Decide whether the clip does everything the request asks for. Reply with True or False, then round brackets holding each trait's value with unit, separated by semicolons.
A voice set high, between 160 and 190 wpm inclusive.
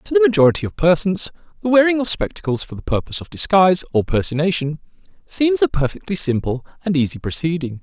False (175 Hz; 175 wpm)